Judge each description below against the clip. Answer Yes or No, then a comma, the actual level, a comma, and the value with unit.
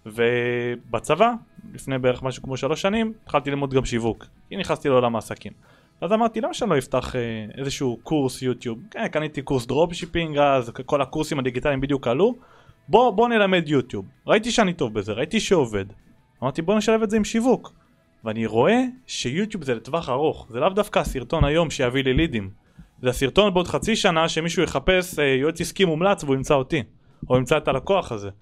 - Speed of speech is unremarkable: No, fast, 175 wpm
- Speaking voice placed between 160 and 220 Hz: No, medium, 145 Hz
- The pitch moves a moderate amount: No, wide, 6.6 semitones